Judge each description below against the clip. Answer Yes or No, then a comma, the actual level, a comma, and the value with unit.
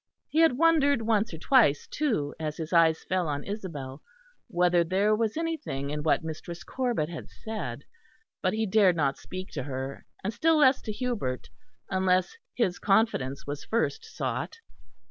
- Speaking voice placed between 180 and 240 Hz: Yes, medium, 185 Hz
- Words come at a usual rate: Yes, average, 165 wpm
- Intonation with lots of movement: Yes, wide, 7.3 semitones